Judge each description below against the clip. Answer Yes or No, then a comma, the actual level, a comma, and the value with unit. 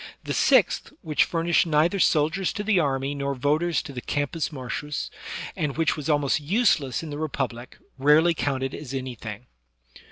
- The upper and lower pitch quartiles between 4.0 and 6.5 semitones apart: No, average, 3.3 semitones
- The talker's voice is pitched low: No, medium, 150 Hz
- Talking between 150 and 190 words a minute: Yes, average, 160 wpm